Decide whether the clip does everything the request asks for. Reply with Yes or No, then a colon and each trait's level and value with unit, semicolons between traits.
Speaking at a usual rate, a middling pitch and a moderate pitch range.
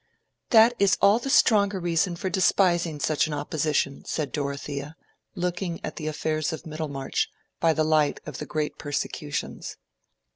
Yes: average, 150 wpm; medium, 160 Hz; average, 3.4 semitones